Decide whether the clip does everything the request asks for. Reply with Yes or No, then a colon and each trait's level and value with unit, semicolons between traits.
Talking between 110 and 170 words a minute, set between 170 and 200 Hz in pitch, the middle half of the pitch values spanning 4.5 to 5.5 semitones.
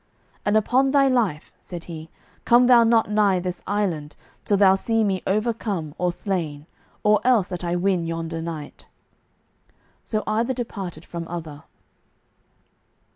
Yes: average, 140 wpm; high, 190 Hz; average, 4.8 semitones